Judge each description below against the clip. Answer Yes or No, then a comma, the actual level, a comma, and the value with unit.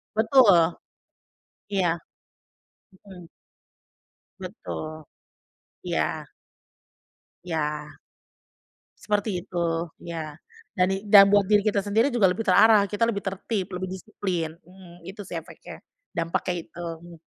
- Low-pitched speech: No, high, 190 Hz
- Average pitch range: Yes, average, 3.2 semitones